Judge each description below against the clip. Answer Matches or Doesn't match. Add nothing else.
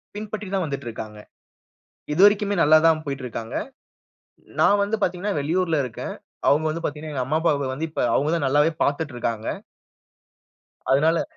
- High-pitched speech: Doesn't match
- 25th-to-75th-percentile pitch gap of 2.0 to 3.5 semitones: Doesn't match